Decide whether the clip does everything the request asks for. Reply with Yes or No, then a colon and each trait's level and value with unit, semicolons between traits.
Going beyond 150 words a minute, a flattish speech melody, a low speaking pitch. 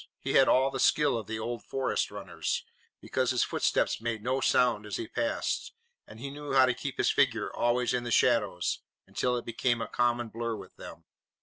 Yes: fast, 205 wpm; narrow, 2.3 semitones; low, 120 Hz